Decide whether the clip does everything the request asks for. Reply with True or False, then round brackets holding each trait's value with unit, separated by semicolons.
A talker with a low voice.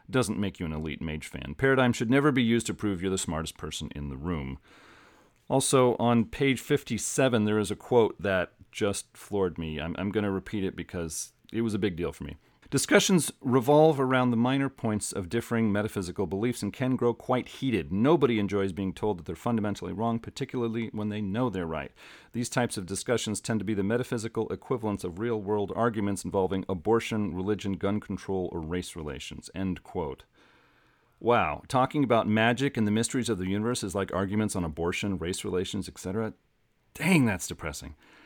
True (105 Hz)